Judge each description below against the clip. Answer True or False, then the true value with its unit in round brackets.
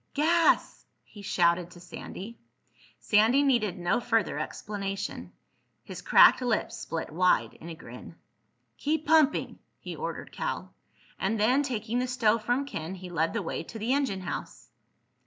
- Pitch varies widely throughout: True (5.8 semitones)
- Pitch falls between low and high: False (215 Hz)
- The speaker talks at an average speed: True (150 wpm)